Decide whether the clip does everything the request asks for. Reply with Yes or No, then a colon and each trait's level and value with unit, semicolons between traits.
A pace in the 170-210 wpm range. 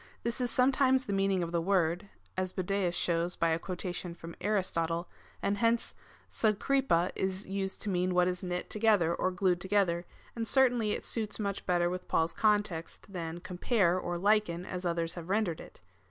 Yes: average, 180 wpm